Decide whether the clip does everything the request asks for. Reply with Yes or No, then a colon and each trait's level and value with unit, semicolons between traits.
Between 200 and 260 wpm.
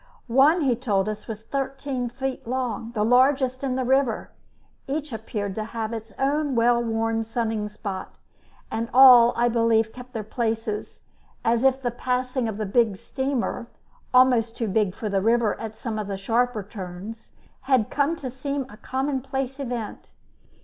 No: average, 165 wpm